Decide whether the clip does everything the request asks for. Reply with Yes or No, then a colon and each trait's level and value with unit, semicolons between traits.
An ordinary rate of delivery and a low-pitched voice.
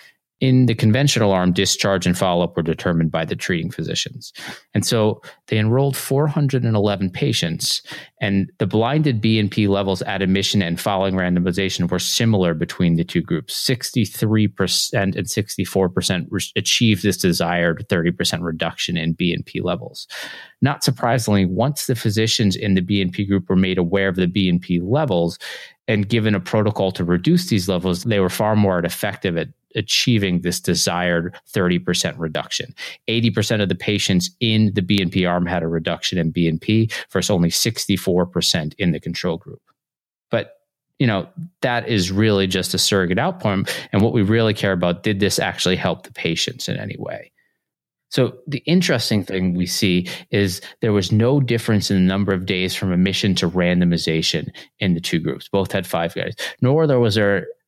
Yes: average, 170 wpm; low, 100 Hz